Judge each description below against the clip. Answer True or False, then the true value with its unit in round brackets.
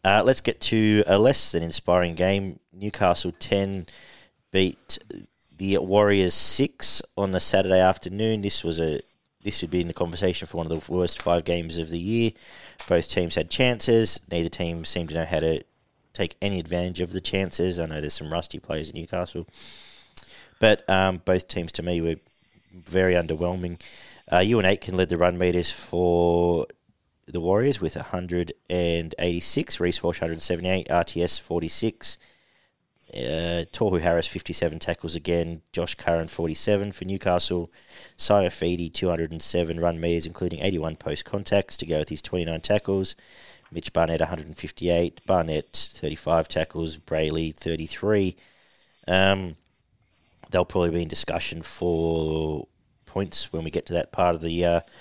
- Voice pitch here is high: False (85 Hz)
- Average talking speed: True (155 wpm)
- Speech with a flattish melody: True (2.1 semitones)